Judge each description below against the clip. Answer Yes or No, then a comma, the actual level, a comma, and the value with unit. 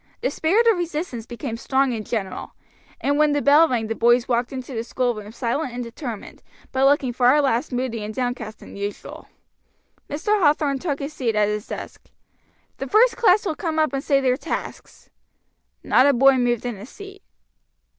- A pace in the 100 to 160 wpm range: No, average, 185 wpm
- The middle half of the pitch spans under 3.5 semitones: No, average, 4.3 semitones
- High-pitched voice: Yes, very high, 260 Hz